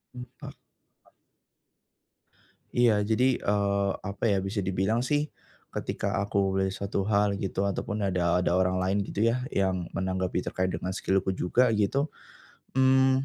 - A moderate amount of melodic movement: Yes, average, 3.4 semitones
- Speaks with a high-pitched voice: No, low, 100 Hz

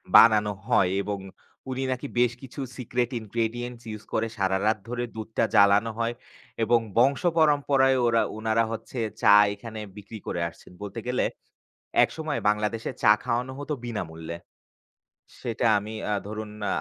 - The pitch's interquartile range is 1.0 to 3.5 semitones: Yes, average, 2.8 semitones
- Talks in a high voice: No, low, 115 Hz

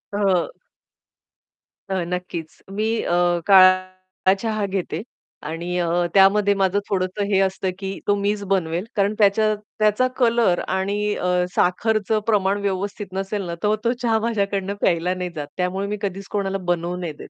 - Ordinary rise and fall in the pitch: No, narrow, 2.0 semitones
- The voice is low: No, high, 195 Hz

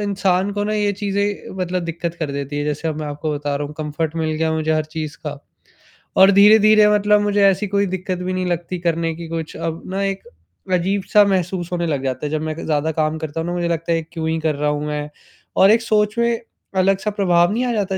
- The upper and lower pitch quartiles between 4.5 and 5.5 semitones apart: No, average, 4.1 semitones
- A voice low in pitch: No, medium, 170 Hz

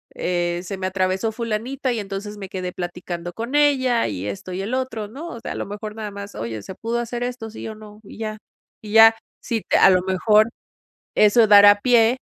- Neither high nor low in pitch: No, high, 210 Hz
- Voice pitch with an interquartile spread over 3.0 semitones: Yes, average, 3.5 semitones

